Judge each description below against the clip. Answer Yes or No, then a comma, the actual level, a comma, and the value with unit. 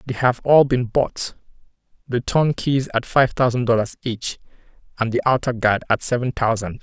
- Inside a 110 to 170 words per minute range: Yes, average, 160 wpm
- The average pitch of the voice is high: No, low, 120 Hz